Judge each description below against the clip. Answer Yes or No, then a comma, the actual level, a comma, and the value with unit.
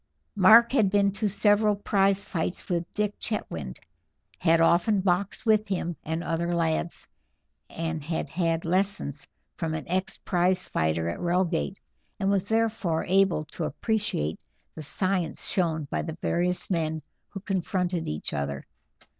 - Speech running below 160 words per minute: Yes, average, 145 wpm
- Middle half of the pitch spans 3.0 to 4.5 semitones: Yes, average, 3.5 semitones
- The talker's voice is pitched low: No, medium, 180 Hz